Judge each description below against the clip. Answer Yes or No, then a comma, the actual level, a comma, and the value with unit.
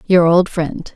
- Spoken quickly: No, average, 190 wpm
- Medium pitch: Yes, medium, 170 Hz